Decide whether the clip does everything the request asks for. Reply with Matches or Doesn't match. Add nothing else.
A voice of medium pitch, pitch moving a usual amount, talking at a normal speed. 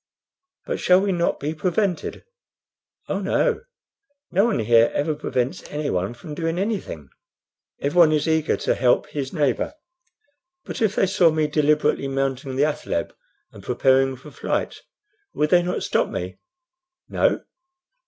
Matches